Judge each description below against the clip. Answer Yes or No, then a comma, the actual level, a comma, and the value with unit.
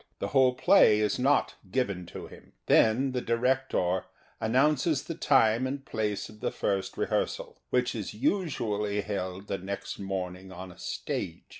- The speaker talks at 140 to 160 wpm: Yes, average, 155 wpm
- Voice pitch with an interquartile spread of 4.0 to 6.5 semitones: Yes, average, 4.9 semitones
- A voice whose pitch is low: Yes, low, 110 Hz